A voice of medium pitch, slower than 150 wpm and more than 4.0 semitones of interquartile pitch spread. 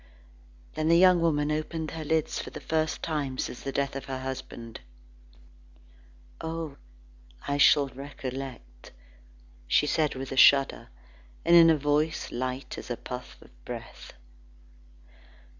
No: medium, 145 Hz; average, 140 wpm; average, 3.1 semitones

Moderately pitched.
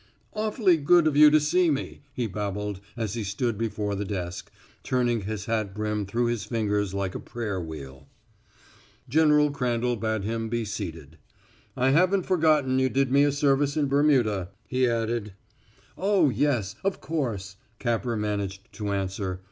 No: low, 115 Hz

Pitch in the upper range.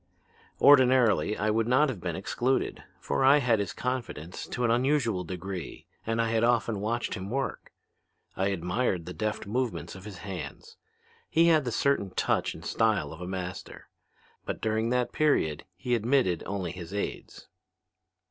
No: low, 110 Hz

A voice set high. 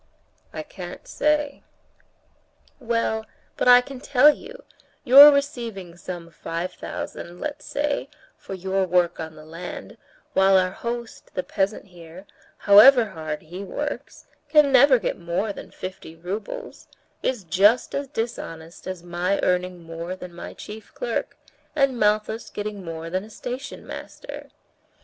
Yes: high, 200 Hz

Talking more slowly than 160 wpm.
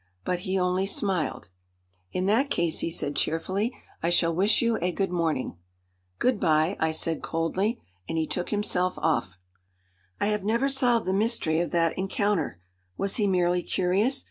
No: average, 170 wpm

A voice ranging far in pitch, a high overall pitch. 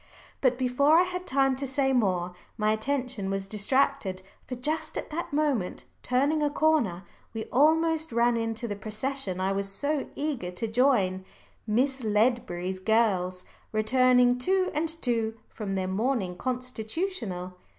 Yes: wide, 5.9 semitones; high, 245 Hz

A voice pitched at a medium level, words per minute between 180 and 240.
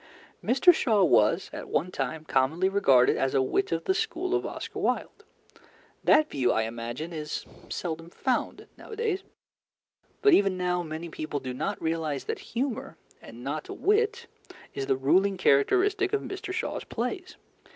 No: medium, 180 Hz; average, 155 wpm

